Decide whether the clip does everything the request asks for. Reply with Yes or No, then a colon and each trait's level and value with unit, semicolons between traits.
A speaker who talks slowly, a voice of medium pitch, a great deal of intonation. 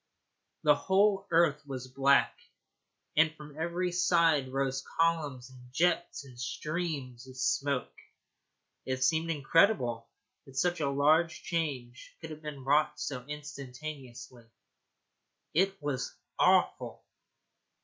No: slow, 110 wpm; medium, 145 Hz; average, 4.1 semitones